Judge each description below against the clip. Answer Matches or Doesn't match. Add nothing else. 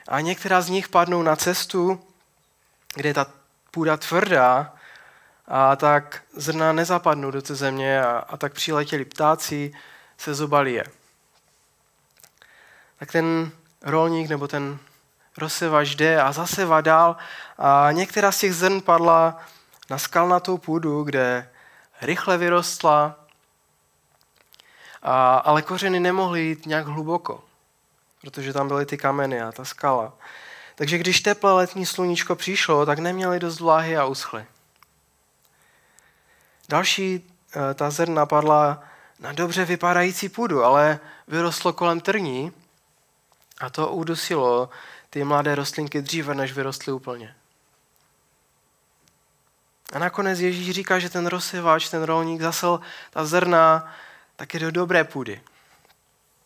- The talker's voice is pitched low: Doesn't match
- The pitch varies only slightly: Doesn't match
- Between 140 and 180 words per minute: Doesn't match